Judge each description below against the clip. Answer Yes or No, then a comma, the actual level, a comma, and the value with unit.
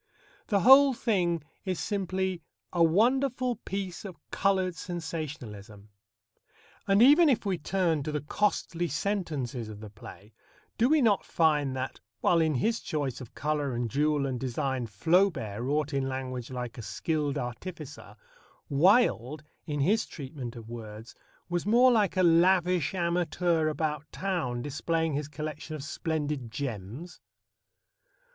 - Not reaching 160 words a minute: Yes, average, 140 wpm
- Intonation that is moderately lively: No, wide, 6.0 semitones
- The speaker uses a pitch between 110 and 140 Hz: No, medium, 155 Hz